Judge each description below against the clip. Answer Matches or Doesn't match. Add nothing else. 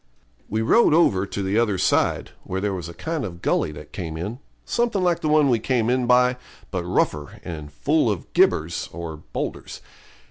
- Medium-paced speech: Matches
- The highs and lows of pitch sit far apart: Matches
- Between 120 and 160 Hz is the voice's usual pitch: Doesn't match